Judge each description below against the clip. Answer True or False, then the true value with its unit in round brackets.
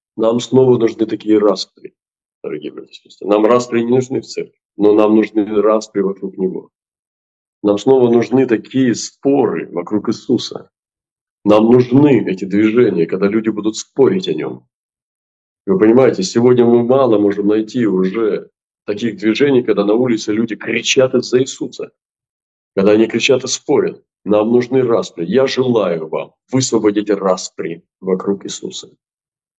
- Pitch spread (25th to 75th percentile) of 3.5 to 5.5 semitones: False (3.0 semitones)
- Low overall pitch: True (110 Hz)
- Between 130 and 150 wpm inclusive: True (140 wpm)